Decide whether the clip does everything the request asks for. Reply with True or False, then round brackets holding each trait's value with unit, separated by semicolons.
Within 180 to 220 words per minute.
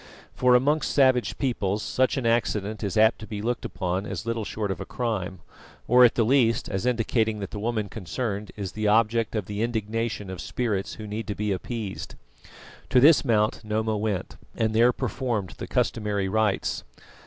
True (185 wpm)